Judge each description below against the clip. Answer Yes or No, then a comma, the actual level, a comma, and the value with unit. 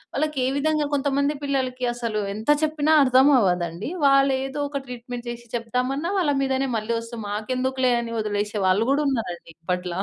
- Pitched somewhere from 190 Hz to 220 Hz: No, very high, 255 Hz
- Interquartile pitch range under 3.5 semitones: No, average, 3.8 semitones